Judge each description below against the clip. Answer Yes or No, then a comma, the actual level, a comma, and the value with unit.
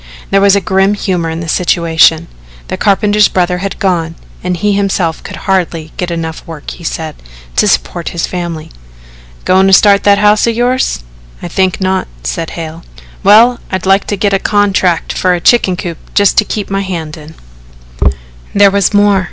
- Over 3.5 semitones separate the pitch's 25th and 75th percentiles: No, average, 3.2 semitones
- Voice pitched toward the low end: No, high, 190 Hz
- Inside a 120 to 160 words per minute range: No, average, 180 wpm